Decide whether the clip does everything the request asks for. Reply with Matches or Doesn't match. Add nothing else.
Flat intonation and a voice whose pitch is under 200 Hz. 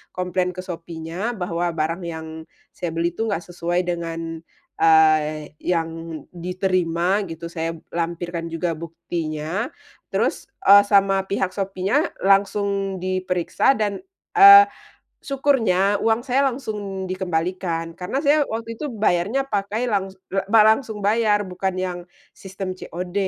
Doesn't match